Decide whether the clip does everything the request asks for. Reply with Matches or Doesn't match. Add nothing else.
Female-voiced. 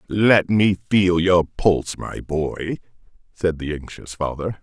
Doesn't match